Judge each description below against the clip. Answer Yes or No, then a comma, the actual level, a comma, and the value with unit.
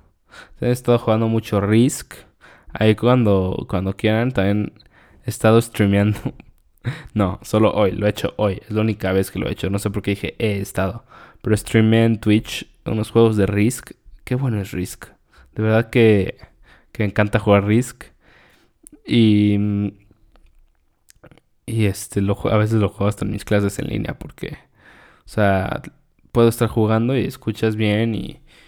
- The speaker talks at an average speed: Yes, average, 165 wpm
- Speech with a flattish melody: Yes, narrow, 2.1 semitones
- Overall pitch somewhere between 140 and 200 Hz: No, low, 105 Hz